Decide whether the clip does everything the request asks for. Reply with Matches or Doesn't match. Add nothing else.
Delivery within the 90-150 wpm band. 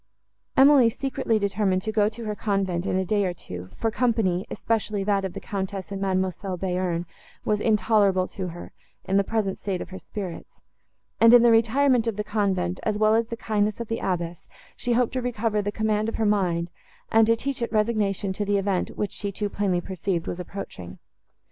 Doesn't match